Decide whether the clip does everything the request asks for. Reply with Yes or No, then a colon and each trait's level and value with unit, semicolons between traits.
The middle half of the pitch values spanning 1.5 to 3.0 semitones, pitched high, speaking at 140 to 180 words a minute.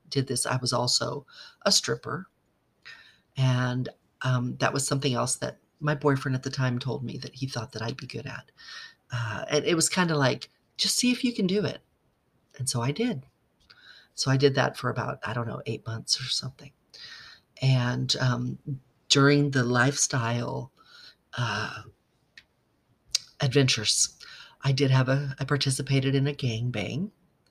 No: narrow, 2.6 semitones; low, 135 Hz; average, 170 wpm